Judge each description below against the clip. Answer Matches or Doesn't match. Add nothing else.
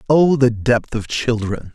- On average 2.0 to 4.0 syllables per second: Matches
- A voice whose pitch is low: Matches